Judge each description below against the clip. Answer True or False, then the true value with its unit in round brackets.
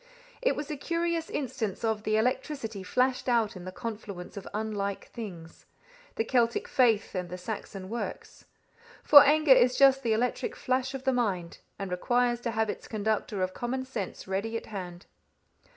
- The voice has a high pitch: True (225 Hz)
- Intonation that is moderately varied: True (4.4 semitones)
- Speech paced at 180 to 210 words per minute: False (170 wpm)